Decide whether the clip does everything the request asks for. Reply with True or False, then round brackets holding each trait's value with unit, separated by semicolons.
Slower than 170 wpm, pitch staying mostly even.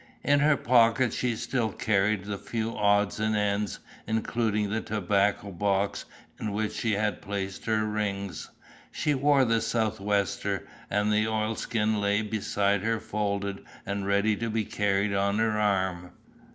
True (150 wpm; 1.8 semitones)